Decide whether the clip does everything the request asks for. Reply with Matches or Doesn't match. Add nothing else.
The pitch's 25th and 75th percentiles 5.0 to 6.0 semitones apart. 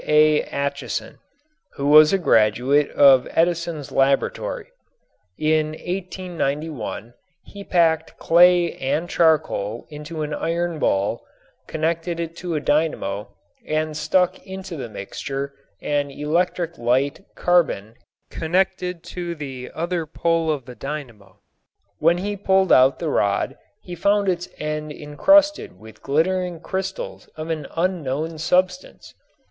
Doesn't match